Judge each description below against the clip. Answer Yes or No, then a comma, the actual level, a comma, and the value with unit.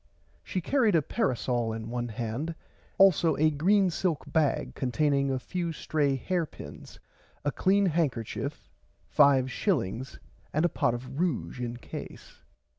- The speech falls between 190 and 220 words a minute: No, average, 140 wpm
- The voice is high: No, medium, 145 Hz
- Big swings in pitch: Yes, wide, 5.8 semitones